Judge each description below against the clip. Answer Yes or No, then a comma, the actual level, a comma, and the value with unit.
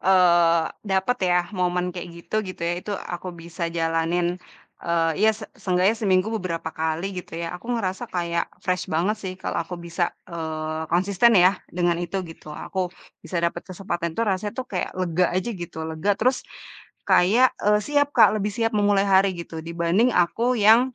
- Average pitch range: Yes, average, 3.2 semitones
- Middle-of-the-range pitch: Yes, medium, 180 Hz